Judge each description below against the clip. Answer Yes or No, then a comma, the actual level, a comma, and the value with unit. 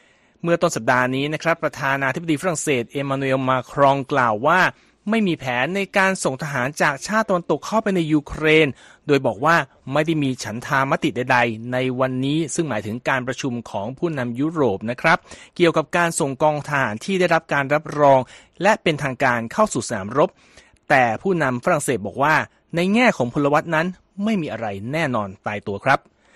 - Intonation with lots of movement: No, average, 4.5 semitones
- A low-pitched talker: No, medium, 145 Hz